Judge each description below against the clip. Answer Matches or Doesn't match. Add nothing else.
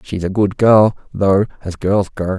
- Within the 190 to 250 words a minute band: Matches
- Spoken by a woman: Doesn't match